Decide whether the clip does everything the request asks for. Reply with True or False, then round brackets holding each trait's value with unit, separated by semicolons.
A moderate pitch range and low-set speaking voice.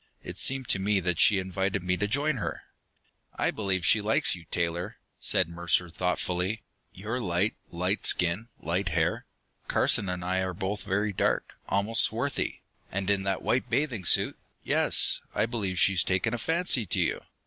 True (3.3 semitones; 95 Hz)